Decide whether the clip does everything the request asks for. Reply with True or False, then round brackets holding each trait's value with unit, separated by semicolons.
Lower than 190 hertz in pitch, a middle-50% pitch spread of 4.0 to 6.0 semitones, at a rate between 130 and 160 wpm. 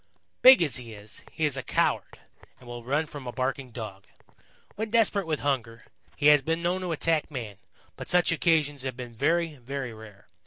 False (140 Hz; 5.2 semitones; 195 wpm)